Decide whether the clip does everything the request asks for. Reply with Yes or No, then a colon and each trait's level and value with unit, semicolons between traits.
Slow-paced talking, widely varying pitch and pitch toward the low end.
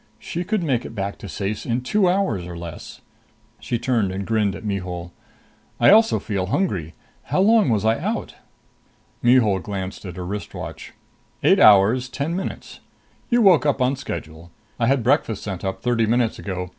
No: average, 180 wpm; wide, 6.2 semitones; low, 110 Hz